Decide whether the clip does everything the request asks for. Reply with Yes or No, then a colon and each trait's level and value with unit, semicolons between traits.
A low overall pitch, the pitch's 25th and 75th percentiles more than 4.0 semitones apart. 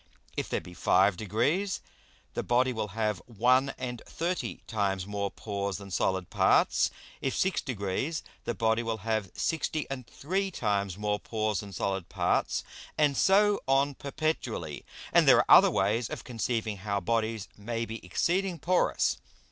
Yes: low, 110 Hz; average, 5.2 semitones